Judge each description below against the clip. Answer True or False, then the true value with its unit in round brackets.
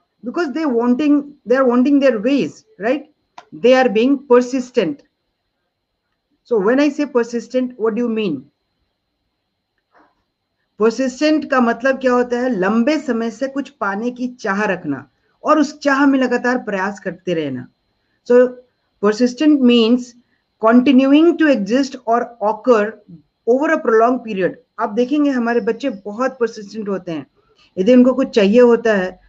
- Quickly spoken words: False (125 wpm)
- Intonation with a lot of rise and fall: False (3.3 semitones)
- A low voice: False (245 Hz)